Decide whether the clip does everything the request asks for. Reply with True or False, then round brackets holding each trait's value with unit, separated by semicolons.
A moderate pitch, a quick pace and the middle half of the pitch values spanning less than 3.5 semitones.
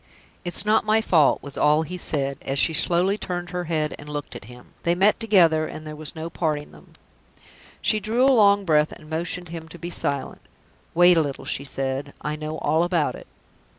True (160 Hz; 210 wpm; 3.1 semitones)